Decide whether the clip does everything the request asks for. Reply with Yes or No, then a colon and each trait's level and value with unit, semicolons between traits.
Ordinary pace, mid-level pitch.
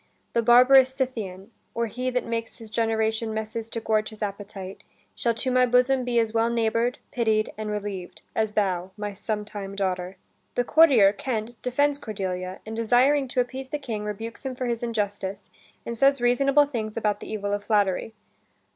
No: average, 175 wpm; high, 225 Hz